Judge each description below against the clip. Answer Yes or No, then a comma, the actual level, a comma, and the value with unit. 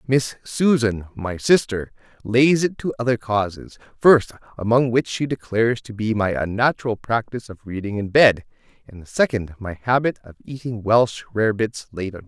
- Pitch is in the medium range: No, low, 115 Hz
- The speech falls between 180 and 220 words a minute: No, average, 170 wpm